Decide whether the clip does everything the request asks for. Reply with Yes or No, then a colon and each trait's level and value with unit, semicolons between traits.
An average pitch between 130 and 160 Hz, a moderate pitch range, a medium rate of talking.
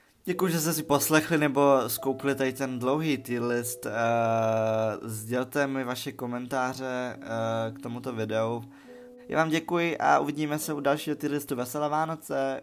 Yes: low, 135 Hz; average, 3.6 semitones; average, 145 wpm